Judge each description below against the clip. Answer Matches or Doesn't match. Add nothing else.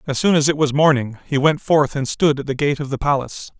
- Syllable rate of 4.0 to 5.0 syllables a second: Doesn't match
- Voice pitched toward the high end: Doesn't match